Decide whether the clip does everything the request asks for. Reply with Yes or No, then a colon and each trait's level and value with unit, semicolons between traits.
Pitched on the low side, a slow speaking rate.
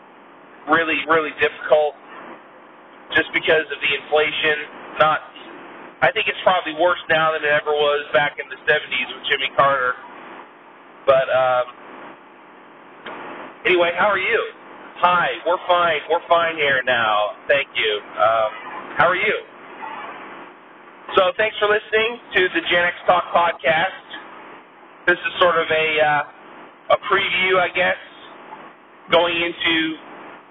No: medium, 165 Hz; slow, 130 wpm